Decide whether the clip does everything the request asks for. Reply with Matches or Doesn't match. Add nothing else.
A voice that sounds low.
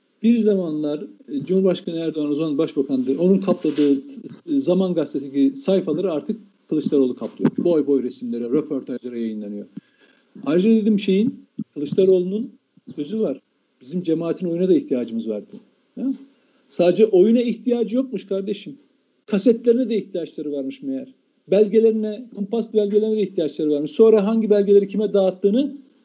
Doesn't match